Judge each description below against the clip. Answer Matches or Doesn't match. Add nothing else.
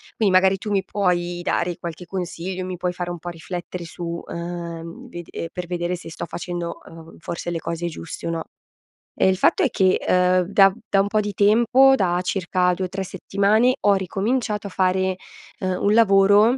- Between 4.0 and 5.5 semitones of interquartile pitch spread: Doesn't match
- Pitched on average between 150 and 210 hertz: Matches